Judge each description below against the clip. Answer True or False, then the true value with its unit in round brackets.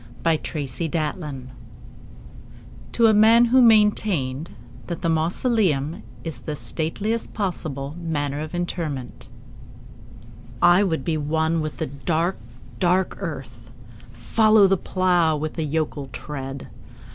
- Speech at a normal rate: False (120 wpm)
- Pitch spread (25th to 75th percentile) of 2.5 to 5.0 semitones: True (4.4 semitones)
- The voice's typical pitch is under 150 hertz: False (160 Hz)